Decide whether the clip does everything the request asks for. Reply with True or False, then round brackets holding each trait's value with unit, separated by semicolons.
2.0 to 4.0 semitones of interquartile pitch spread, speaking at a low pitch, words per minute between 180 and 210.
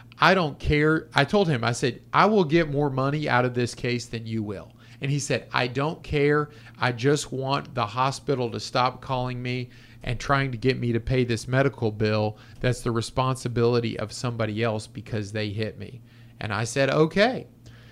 True (3.0 semitones; 125 Hz; 200 wpm)